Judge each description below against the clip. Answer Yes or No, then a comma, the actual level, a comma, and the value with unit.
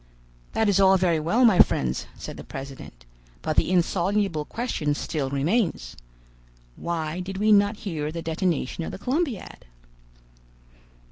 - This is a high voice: No, medium, 175 Hz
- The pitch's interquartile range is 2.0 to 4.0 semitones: No, average, 5.0 semitones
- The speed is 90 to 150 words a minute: Yes, average, 140 wpm